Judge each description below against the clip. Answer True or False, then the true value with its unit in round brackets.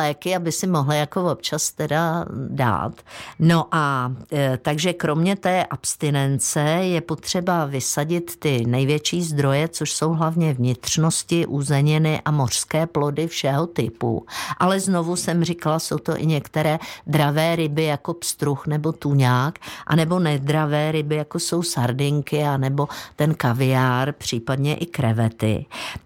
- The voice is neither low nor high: True (150 Hz)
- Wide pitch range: False (2.8 semitones)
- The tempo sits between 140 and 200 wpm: False (130 wpm)